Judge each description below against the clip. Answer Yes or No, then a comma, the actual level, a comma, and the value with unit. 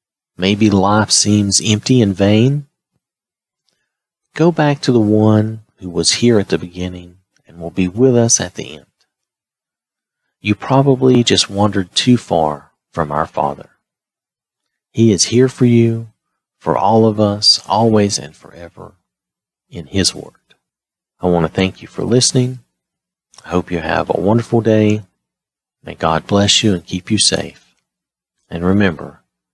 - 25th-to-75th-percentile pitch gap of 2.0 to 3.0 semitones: No, average, 4.4 semitones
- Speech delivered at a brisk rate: No, average, 150 wpm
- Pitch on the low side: Yes, low, 105 Hz